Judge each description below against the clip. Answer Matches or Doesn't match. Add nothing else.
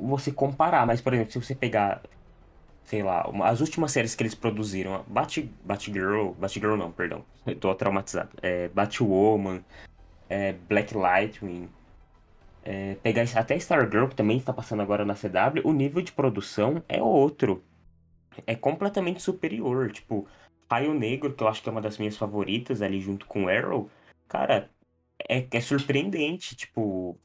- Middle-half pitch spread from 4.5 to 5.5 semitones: Matches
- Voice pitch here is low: Matches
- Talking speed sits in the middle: Matches